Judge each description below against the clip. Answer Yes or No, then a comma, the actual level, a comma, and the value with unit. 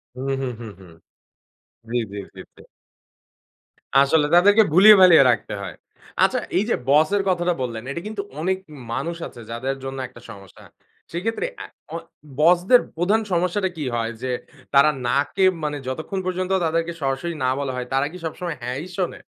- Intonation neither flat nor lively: No, wide, 5.9 semitones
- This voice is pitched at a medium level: Yes, medium, 155 Hz